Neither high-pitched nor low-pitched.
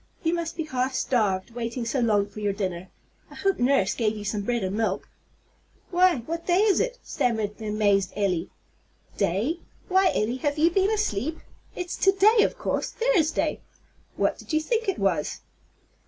No: high, 245 Hz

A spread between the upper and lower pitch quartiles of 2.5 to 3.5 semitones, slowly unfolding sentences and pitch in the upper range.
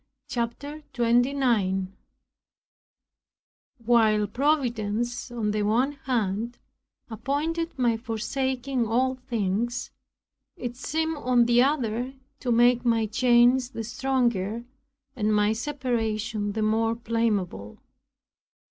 Yes: average, 2.9 semitones; slow, 95 wpm; high, 235 Hz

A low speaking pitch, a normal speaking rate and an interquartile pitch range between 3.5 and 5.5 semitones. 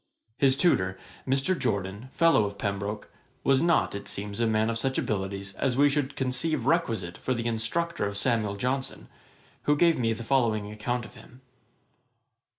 Yes: low, 115 Hz; average, 165 wpm; average, 4.9 semitones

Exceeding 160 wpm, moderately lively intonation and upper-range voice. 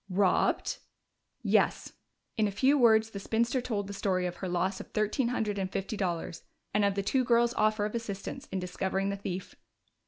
Yes: average, 190 wpm; average, 3.1 semitones; high, 205 Hz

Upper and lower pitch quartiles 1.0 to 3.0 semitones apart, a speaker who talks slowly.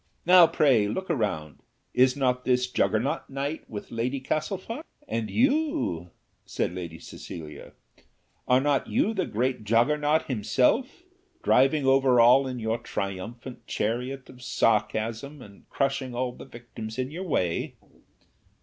No: average, 4.2 semitones; slow, 130 wpm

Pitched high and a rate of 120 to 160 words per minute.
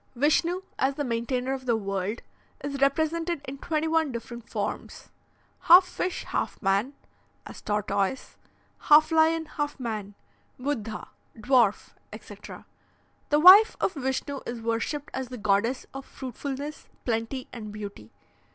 Yes: very high, 265 Hz; slow, 135 wpm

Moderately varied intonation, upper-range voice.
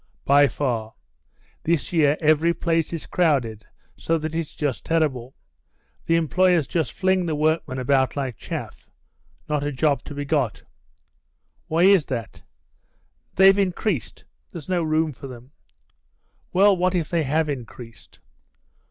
No: average, 3.8 semitones; medium, 155 Hz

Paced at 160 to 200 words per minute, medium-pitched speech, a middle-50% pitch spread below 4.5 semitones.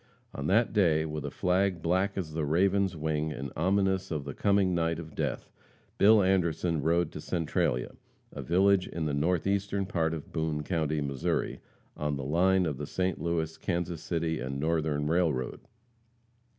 No: average, 165 wpm; very low, 85 Hz; average, 3.4 semitones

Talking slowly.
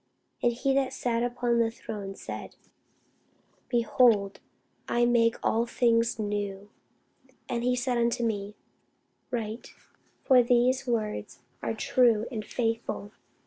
Yes: slow, 120 wpm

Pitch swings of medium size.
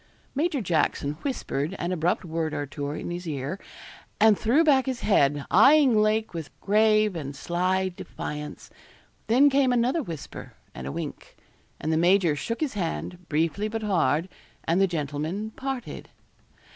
No: wide, 6.1 semitones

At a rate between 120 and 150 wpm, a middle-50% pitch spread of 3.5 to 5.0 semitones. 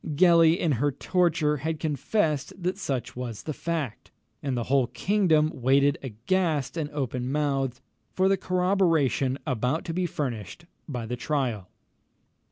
Yes: average, 145 wpm; average, 4.6 semitones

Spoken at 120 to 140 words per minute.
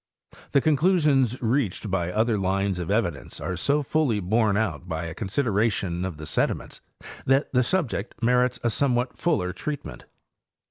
No: average, 155 wpm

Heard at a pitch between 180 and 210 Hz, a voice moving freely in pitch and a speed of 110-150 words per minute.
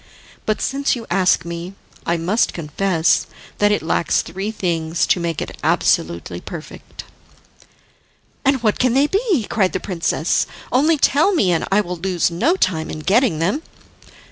No: high, 190 Hz; wide, 6.4 semitones; average, 160 wpm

